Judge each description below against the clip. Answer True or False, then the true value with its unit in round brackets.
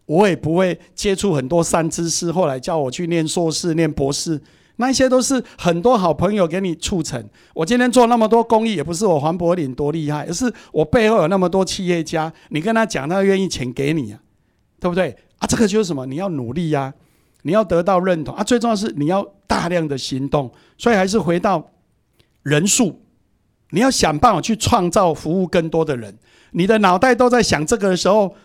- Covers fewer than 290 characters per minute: False (305 characters per minute)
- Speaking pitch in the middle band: True (175 Hz)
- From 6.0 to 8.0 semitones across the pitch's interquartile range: False (5.2 semitones)